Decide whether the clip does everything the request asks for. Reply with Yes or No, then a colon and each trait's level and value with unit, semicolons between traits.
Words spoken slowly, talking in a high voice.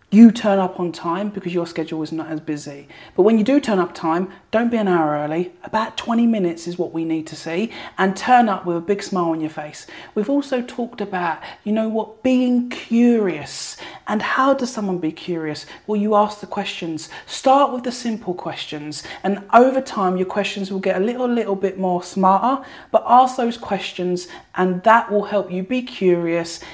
No: fast, 205 wpm; high, 195 Hz